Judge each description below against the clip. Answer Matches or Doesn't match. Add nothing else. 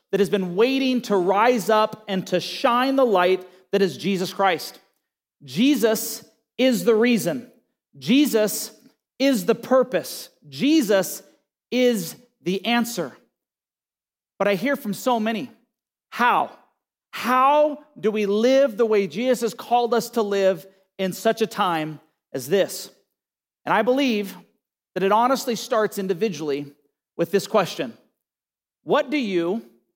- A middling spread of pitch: Matches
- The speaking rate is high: Doesn't match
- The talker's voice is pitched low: Doesn't match